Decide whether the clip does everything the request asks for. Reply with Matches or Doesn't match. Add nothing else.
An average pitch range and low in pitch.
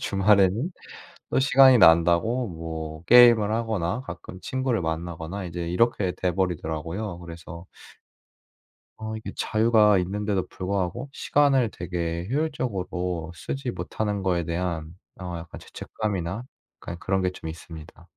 Matches